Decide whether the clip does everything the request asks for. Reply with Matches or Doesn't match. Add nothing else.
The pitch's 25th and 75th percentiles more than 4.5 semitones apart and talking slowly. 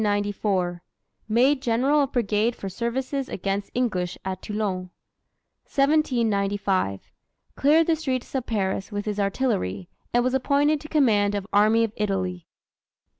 Matches